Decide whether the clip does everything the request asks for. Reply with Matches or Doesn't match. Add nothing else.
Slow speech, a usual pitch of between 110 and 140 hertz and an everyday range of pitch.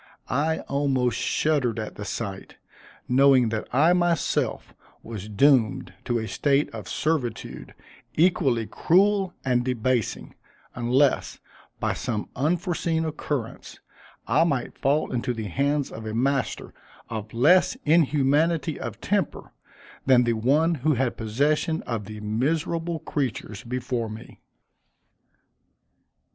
Matches